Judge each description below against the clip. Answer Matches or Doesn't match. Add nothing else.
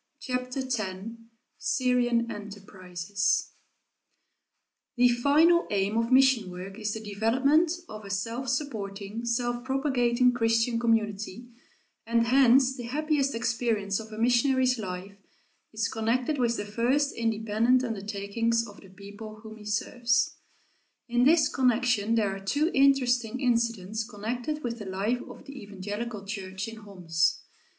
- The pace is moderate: Doesn't match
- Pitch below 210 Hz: Doesn't match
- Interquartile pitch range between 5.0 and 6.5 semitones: Doesn't match